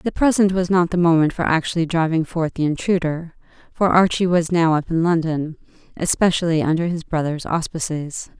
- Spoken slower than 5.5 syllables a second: Yes, 5.3 syllables/s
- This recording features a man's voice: No, female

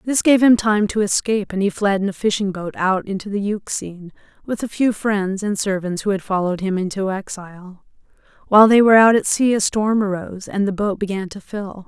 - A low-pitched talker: No, high, 200 Hz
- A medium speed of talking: No, fast, 220 wpm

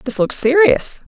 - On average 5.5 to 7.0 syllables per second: No, 4.9 syllables/s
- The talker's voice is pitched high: Yes, very high, 295 Hz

